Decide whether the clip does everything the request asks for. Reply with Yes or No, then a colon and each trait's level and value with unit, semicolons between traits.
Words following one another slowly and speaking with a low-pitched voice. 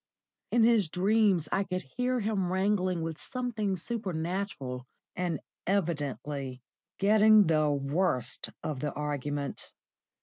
No: slow, 110 wpm; medium, 180 Hz